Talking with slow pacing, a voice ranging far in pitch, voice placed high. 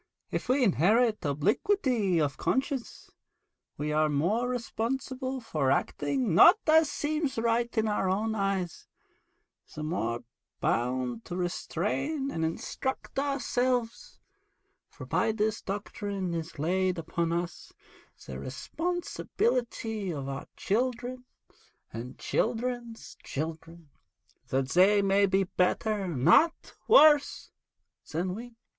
Yes: slow, 115 wpm; wide, 7.0 semitones; high, 205 Hz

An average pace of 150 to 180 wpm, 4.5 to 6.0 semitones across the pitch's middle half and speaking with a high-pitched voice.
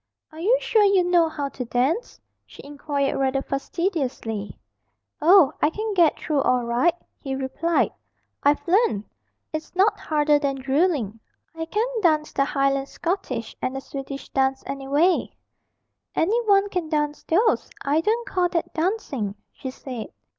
Yes: average, 155 wpm; average, 4.8 semitones; very high, 300 Hz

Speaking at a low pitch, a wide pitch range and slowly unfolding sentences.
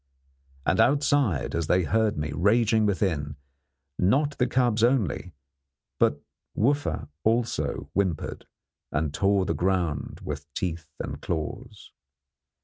Yes: low, 100 Hz; wide, 6.2 semitones; slow, 115 wpm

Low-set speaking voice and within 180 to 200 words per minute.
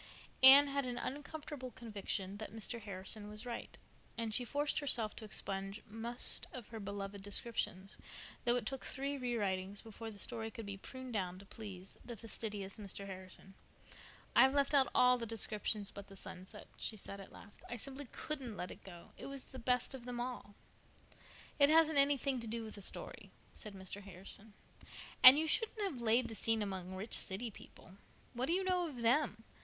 No: high, 225 Hz; average, 190 wpm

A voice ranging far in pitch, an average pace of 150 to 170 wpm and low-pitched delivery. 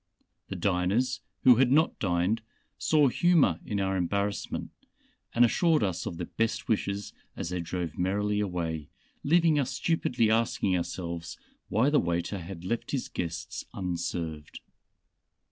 No: wide, 5.8 semitones; average, 140 wpm; low, 100 Hz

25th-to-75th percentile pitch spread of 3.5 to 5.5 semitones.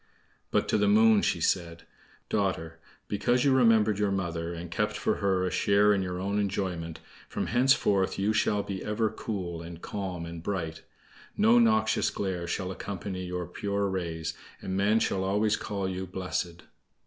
No: average, 2.9 semitones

